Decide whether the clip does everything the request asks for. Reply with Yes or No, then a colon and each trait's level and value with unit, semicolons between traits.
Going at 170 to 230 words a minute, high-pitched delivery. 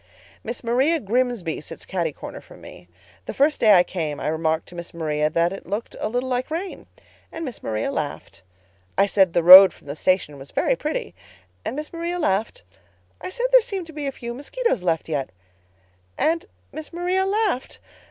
Yes: average, 180 wpm; high, 205 Hz